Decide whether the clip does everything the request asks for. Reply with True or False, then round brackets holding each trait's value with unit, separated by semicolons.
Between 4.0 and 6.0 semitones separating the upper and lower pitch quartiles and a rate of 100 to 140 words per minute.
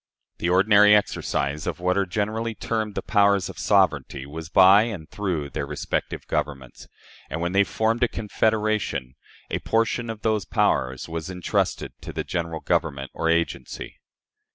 False (4.9 semitones; 155 wpm)